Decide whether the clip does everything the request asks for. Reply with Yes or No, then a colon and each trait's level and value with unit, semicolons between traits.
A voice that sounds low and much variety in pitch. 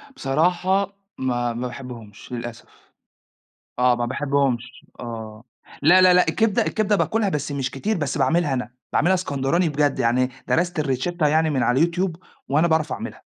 No: medium, 145 Hz; wide, 5.8 semitones